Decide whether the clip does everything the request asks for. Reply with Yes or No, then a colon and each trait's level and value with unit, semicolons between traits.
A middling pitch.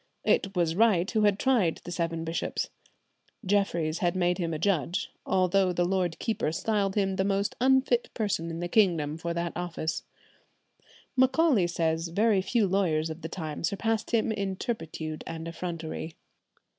Yes: medium, 180 Hz